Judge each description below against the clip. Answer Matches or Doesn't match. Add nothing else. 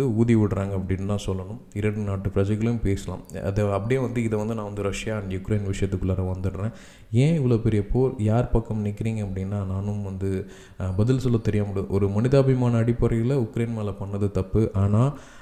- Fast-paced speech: Matches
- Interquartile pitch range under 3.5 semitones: Matches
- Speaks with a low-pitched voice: Matches